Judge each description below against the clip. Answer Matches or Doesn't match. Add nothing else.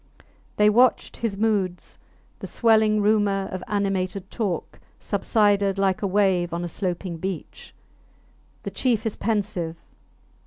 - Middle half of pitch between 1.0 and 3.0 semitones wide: Matches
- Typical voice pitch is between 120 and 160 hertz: Doesn't match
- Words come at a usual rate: Doesn't match